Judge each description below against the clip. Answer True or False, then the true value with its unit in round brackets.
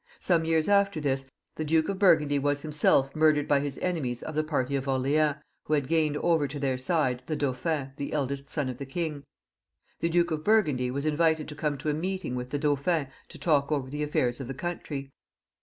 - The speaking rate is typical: False (215 wpm)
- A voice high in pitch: False (150 Hz)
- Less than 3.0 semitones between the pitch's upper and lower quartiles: True (2.6 semitones)